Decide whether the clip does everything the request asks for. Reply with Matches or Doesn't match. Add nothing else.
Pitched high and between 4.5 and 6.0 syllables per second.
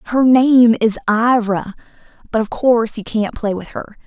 Doesn't match